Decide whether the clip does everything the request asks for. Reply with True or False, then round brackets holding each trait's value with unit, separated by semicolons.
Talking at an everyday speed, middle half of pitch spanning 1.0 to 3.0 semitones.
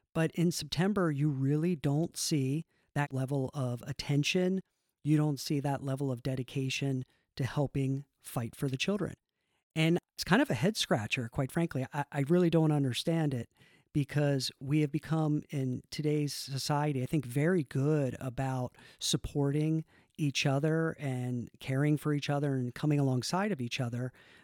True (160 wpm; 2.7 semitones)